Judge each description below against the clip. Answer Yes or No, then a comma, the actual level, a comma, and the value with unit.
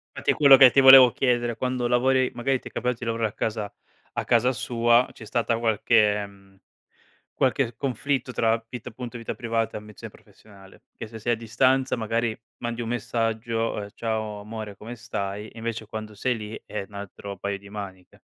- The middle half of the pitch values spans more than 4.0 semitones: No, narrow, 2.4 semitones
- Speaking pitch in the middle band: No, low, 115 Hz